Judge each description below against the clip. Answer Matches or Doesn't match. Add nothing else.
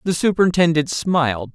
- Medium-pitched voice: Matches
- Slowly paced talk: Matches